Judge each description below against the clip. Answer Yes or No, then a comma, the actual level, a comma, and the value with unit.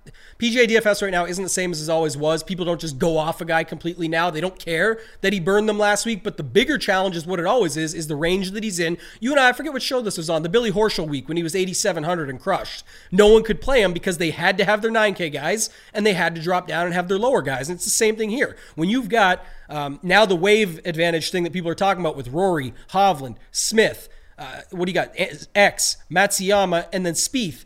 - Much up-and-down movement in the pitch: No, average, 3.8 semitones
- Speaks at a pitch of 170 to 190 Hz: Yes, medium, 185 Hz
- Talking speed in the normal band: No, fast, 265 wpm